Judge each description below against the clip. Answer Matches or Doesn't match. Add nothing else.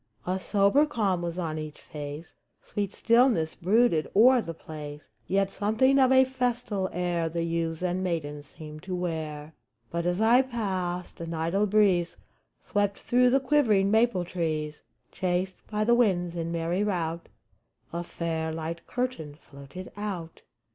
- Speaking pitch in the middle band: Matches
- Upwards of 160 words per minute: Doesn't match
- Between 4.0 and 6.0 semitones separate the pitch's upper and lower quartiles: Matches